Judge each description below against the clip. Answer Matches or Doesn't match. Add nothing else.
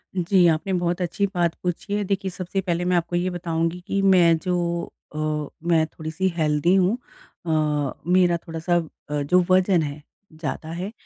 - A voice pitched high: Doesn't match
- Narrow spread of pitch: Matches